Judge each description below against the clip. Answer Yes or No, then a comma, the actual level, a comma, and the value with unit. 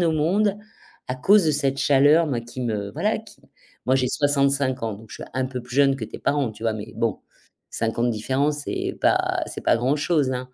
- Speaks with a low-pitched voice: Yes, low, 130 Hz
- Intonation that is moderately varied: Yes, average, 3.7 semitones